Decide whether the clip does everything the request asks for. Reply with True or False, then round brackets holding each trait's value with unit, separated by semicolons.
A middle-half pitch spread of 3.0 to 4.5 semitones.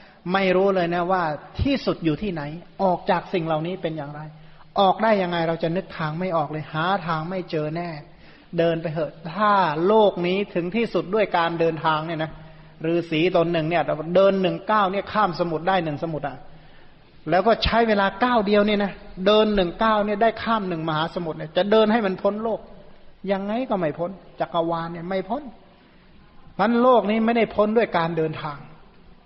True (3.8 semitones)